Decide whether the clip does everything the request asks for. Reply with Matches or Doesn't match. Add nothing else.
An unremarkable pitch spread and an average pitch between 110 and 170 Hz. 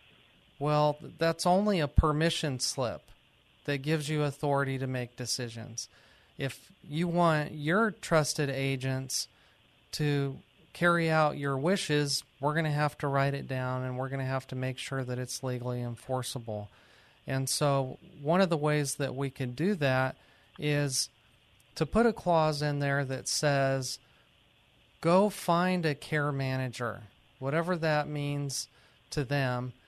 Matches